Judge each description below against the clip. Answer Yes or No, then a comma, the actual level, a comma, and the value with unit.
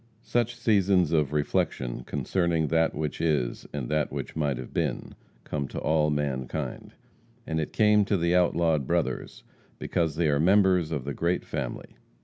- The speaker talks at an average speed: Yes, average, 160 wpm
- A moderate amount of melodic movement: Yes, average, 3.5 semitones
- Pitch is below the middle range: Yes, very low, 80 Hz